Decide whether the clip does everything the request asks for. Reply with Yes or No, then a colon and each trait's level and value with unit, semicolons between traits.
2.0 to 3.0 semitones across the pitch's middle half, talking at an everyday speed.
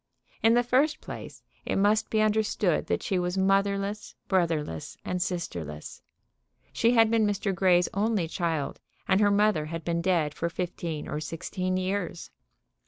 No: average, 3.6 semitones; average, 155 wpm